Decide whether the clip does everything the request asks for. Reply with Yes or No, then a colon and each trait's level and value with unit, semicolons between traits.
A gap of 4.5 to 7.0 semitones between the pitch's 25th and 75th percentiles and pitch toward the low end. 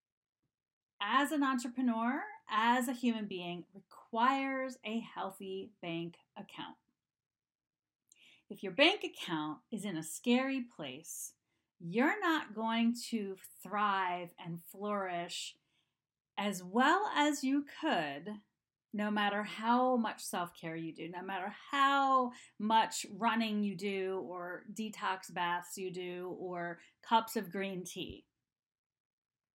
No: wide, 5.5 semitones; high, 210 Hz